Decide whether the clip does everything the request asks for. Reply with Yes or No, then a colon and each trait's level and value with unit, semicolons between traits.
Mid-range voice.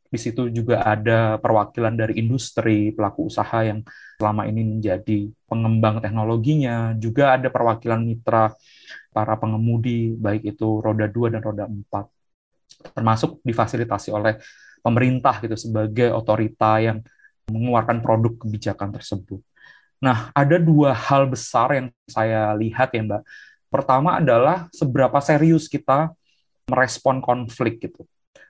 No: low, 115 Hz